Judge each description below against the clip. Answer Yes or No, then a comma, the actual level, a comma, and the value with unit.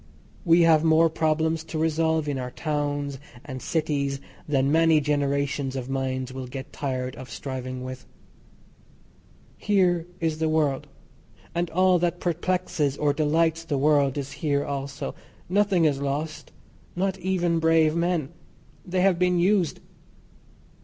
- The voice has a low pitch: No, medium, 155 Hz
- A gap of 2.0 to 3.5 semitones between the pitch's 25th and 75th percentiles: Yes, average, 3.2 semitones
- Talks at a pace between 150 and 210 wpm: No, average, 140 wpm